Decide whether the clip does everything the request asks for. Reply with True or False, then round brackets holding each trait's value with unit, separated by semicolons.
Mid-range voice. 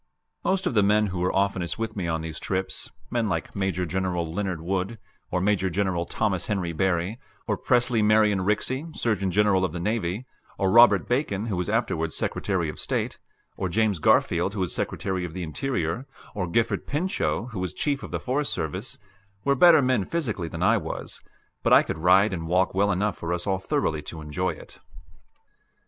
False (95 Hz)